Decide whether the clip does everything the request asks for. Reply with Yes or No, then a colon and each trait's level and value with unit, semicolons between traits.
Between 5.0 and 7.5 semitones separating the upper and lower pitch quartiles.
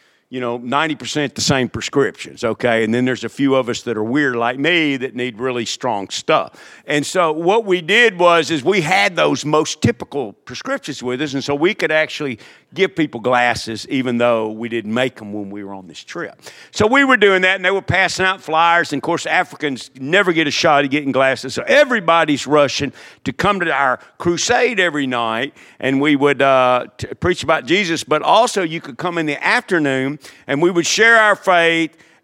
Yes: wide, 5.4 semitones